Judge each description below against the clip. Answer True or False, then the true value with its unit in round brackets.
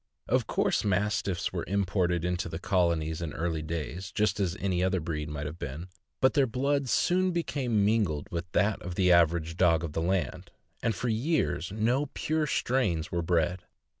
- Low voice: True (90 Hz)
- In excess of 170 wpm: True (180 wpm)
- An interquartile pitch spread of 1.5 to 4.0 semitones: False (4.5 semitones)